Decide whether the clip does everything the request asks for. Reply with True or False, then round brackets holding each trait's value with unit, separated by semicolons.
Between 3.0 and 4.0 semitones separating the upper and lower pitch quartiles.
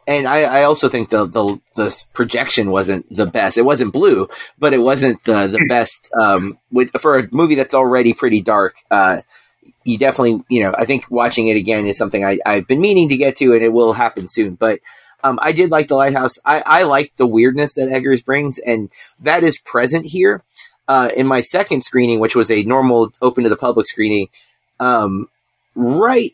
True (3.5 semitones)